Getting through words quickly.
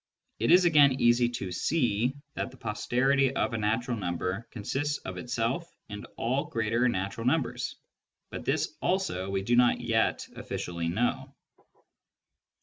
No: average, 145 wpm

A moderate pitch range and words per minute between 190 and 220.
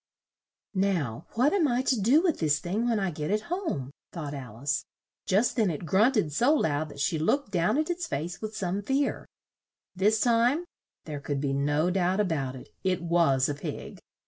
No: wide, 7.9 semitones; average, 200 wpm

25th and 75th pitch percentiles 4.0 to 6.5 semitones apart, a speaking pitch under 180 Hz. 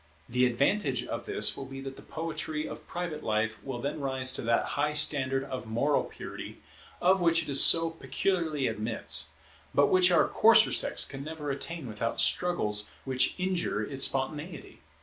Yes: average, 4.5 semitones; medium, 140 Hz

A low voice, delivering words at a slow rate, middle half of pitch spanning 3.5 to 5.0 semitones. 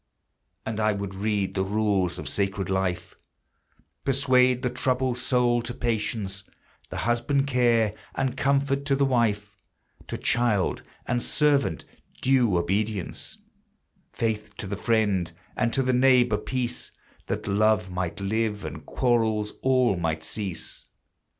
Yes: low, 110 Hz; slow, 130 wpm; average, 4.1 semitones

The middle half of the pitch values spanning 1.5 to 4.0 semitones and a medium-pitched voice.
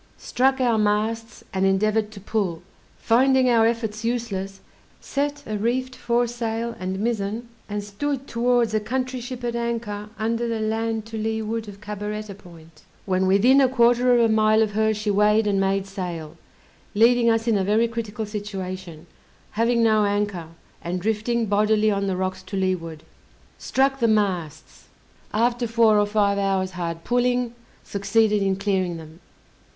No: average, 2.9 semitones; high, 215 Hz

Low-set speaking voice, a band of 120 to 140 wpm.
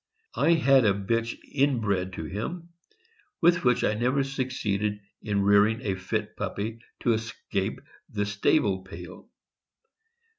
Yes: low, 110 Hz; slow, 135 wpm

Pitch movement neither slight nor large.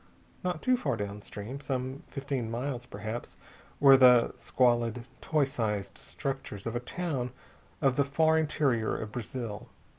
Yes: average, 3.5 semitones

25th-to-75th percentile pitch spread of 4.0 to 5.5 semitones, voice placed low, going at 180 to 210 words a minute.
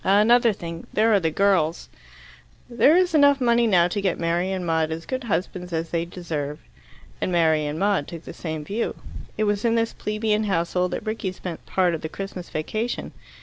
No: average, 4.6 semitones; medium, 185 Hz; average, 195 wpm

